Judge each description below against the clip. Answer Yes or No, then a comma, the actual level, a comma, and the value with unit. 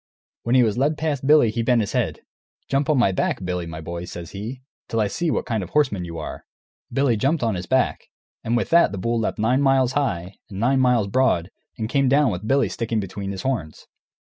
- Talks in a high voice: No, low, 115 Hz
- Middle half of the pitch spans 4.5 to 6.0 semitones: Yes, wide, 5.6 semitones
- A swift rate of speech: Yes, fast, 235 wpm